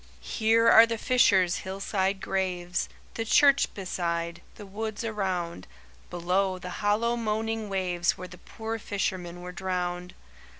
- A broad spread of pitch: No, average, 3.6 semitones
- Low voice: No, high, 190 Hz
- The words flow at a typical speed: No, slow, 130 wpm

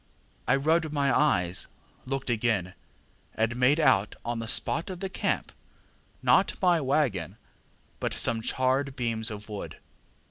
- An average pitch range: Yes, average, 5.0 semitones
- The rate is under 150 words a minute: Yes, average, 140 wpm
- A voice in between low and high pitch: No, low, 125 Hz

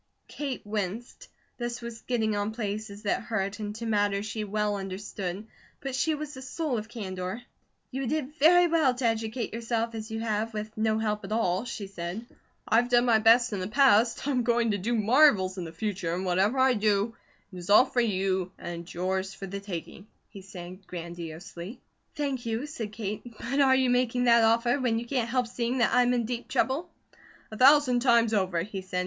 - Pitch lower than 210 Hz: No, high, 220 Hz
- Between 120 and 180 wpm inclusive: No, average, 200 wpm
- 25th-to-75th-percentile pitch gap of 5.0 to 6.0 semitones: No, average, 3.7 semitones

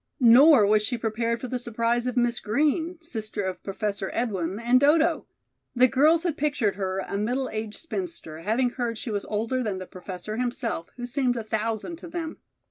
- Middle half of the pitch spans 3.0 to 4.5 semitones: Yes, average, 4.0 semitones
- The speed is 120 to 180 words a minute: No, average, 190 wpm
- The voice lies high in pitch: Yes, high, 235 Hz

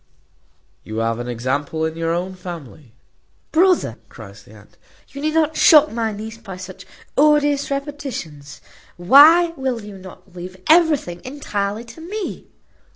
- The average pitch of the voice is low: No, high, 205 Hz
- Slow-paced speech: No, average, 145 wpm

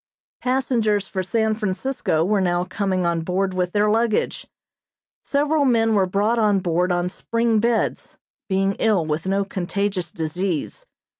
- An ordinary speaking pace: Yes, average, 145 wpm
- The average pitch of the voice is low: No, high, 195 Hz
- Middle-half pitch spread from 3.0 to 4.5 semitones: Yes, average, 3.7 semitones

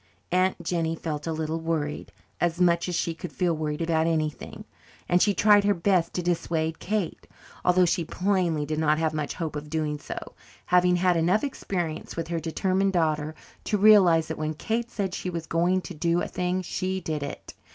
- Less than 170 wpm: No, average, 195 wpm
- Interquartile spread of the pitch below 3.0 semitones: Yes, narrow, 2.5 semitones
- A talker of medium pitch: Yes, medium, 170 Hz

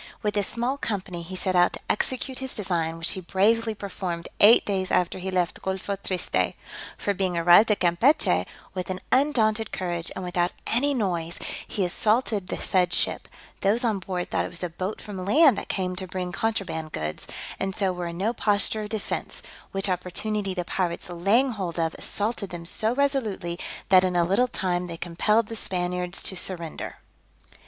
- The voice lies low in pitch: No, high, 190 Hz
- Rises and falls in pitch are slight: No, average, 3.3 semitones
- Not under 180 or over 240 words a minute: Yes, average, 185 wpm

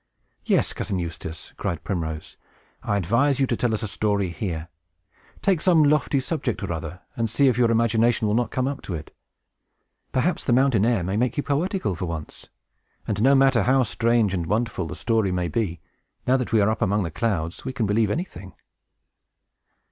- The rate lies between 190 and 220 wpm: Yes, average, 195 wpm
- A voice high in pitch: No, low, 110 Hz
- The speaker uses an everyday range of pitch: No, wide, 5.7 semitones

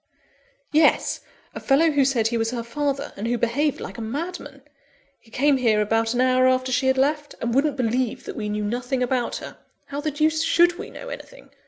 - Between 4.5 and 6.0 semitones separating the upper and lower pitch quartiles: No, average, 3.9 semitones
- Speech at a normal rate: No, fast, 210 wpm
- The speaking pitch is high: Yes, very high, 260 Hz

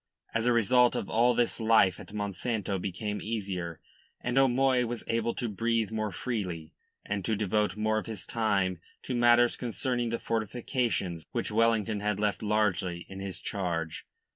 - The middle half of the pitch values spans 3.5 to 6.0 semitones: No, average, 3.1 semitones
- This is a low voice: Yes, low, 110 Hz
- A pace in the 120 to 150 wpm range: No, average, 165 wpm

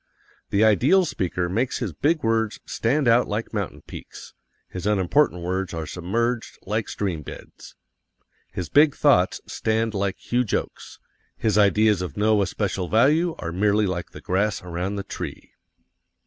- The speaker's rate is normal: Yes, average, 150 wpm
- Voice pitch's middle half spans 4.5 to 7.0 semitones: No, average, 4.0 semitones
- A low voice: Yes, low, 105 Hz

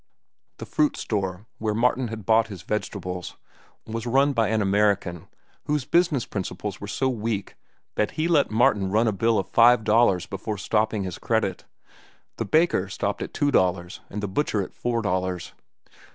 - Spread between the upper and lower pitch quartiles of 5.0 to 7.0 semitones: No, average, 3.5 semitones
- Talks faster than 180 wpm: No, average, 170 wpm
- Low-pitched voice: Yes, low, 105 Hz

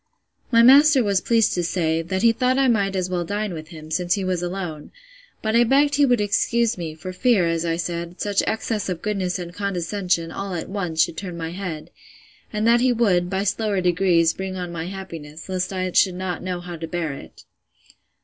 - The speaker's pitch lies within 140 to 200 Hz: Yes, medium, 185 Hz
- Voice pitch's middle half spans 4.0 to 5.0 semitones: No, average, 3.5 semitones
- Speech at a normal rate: No, fast, 210 wpm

